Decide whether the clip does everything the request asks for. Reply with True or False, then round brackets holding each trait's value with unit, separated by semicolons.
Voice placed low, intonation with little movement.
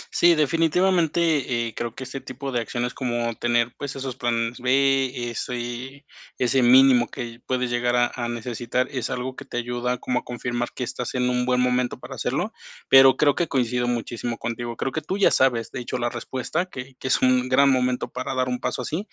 True (125 Hz; 1.8 semitones)